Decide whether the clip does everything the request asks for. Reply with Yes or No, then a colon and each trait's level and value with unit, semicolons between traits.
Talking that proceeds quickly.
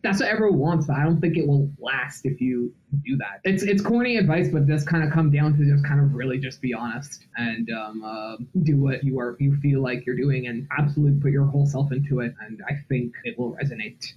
Yes: fast, 250 wpm